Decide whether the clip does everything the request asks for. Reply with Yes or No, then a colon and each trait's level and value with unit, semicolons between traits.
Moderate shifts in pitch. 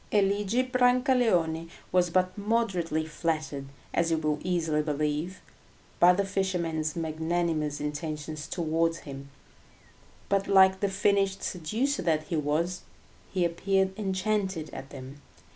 Yes: average, 3.9 semitones